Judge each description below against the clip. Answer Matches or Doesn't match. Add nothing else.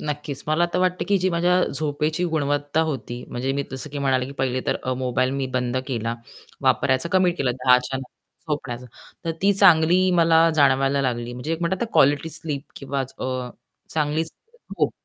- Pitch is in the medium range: Matches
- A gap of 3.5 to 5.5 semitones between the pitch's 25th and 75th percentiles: Matches